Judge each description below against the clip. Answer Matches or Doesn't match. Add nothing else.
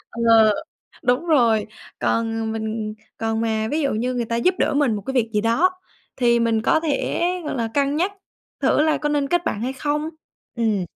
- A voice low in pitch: Doesn't match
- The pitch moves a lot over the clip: Doesn't match